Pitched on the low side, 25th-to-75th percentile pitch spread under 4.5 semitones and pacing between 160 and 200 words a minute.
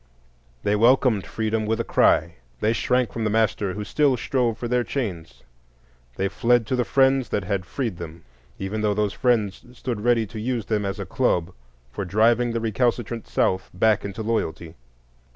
Yes: low, 110 Hz; average, 3.3 semitones; average, 180 wpm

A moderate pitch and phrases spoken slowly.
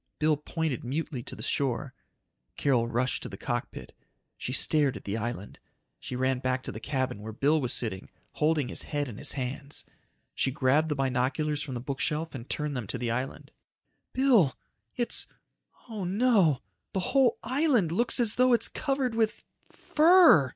No: medium, 145 Hz; average, 170 wpm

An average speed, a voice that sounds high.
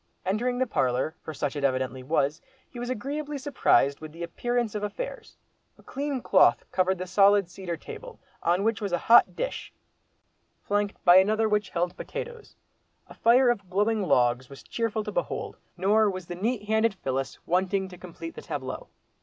Yes: average, 175 wpm; high, 195 Hz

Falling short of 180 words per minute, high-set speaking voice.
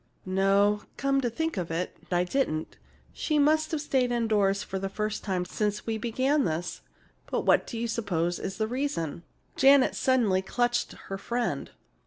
Yes: average, 170 wpm; high, 215 Hz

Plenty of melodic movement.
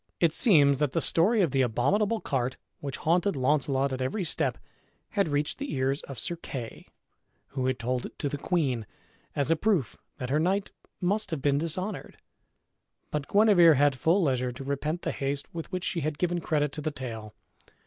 No: average, 4.7 semitones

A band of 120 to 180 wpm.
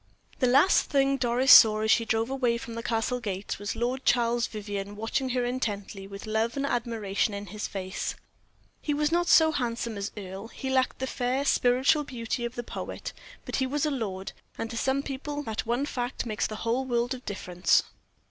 No: average, 200 wpm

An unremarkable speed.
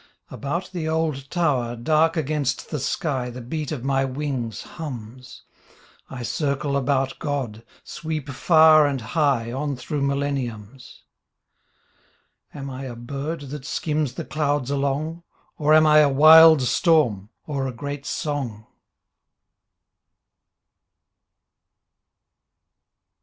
No: slow, 115 wpm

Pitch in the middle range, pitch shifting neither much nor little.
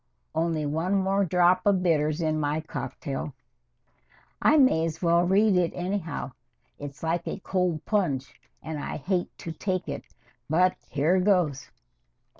Yes: medium, 170 Hz; average, 3.3 semitones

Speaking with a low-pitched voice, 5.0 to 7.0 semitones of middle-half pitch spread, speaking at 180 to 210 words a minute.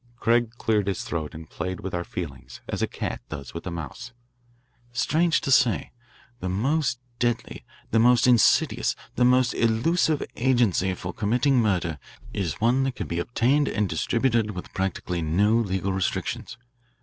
No: low, 110 Hz; average, 5.3 semitones; average, 160 wpm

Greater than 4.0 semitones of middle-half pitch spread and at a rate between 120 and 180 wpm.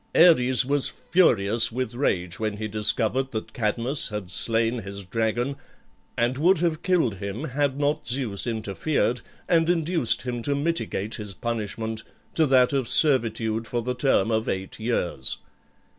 Yes: average, 4.4 semitones; average, 150 wpm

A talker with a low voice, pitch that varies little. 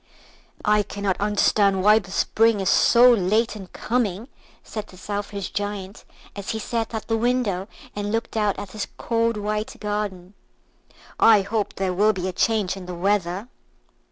No: high, 205 Hz; narrow, 2.2 semitones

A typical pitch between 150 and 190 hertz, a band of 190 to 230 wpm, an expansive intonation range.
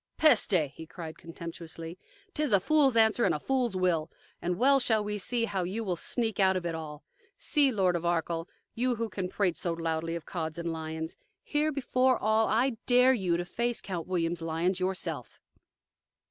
Yes: medium, 185 Hz; average, 195 wpm; wide, 5.7 semitones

